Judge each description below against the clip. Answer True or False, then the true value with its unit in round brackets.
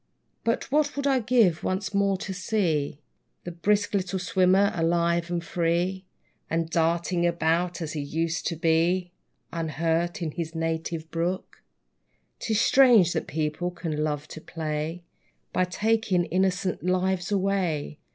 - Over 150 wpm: False (140 wpm)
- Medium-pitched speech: True (175 Hz)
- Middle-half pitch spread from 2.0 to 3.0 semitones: True (2.7 semitones)